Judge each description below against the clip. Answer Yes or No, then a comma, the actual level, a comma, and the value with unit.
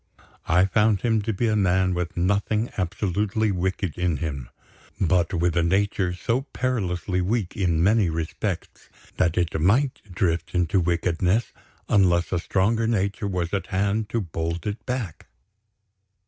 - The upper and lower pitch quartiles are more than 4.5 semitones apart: No, average, 3.4 semitones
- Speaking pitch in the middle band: No, very low, 95 Hz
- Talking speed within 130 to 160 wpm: Yes, average, 145 wpm